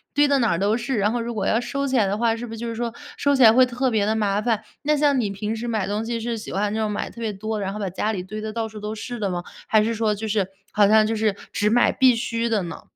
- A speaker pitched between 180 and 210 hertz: No, high, 220 Hz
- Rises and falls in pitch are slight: Yes, narrow, 2.1 semitones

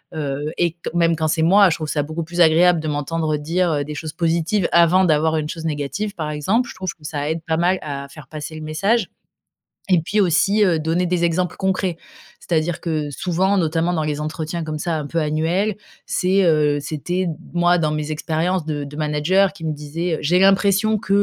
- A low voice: No, medium, 165 Hz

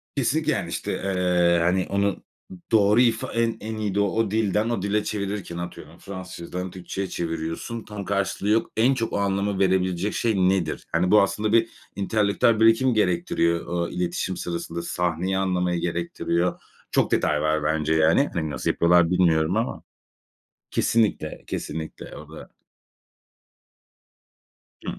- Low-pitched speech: Yes, very low, 95 Hz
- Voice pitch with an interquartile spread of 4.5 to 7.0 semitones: No, average, 3.6 semitones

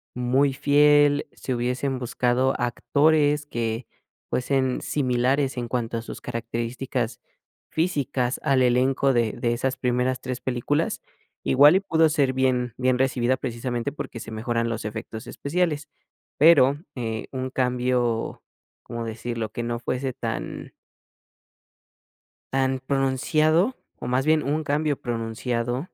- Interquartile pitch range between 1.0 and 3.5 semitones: Yes, average, 2.9 semitones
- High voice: No, low, 130 Hz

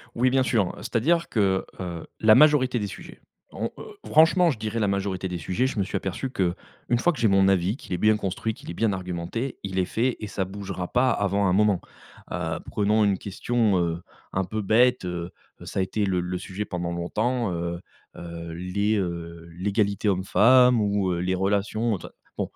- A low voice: Yes, low, 100 Hz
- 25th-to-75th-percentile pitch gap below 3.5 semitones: No, average, 3.8 semitones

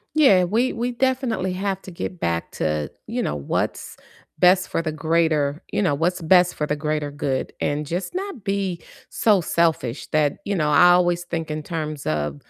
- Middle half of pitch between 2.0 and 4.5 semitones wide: Yes, average, 4.2 semitones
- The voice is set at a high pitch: No, medium, 170 Hz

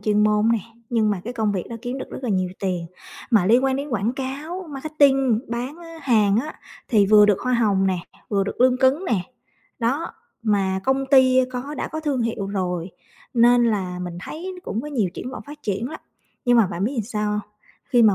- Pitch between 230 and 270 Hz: Yes, high, 235 Hz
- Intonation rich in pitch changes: No, average, 4.6 semitones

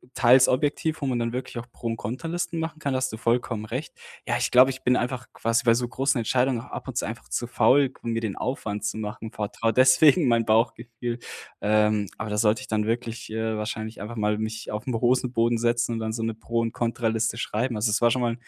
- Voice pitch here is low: Yes, low, 115 Hz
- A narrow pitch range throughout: Yes, narrow, 2.3 semitones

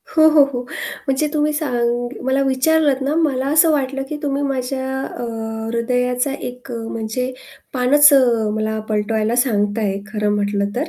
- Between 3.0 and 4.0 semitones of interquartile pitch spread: Yes, average, 3.6 semitones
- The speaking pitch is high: Yes, very high, 255 Hz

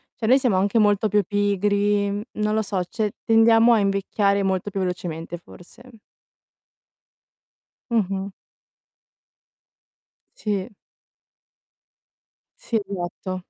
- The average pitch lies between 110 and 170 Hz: No, high, 205 Hz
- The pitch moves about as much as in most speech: No, narrow, 2.3 semitones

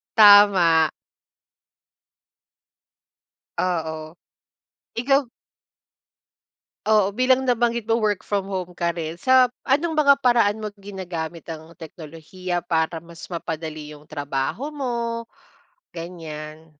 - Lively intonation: Yes, wide, 6.2 semitones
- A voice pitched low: No, medium, 185 Hz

